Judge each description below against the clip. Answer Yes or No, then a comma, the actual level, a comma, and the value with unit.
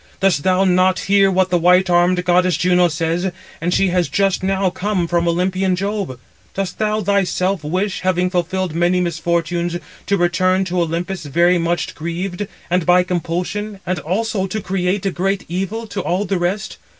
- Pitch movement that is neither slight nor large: No, narrow, 1.8 semitones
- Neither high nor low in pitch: Yes, medium, 180 Hz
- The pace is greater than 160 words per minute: Yes, average, 175 wpm